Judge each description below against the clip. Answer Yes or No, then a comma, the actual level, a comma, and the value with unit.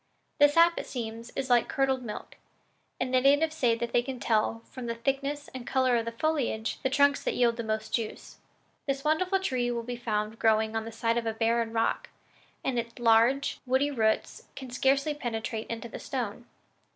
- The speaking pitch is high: Yes, high, 240 Hz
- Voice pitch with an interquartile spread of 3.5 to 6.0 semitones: No, average, 3.1 semitones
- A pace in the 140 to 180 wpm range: No, average, 200 wpm